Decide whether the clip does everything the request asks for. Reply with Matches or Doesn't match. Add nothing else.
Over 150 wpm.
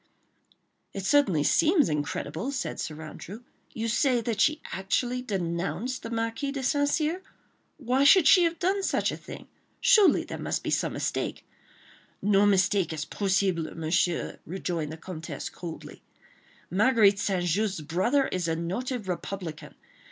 Doesn't match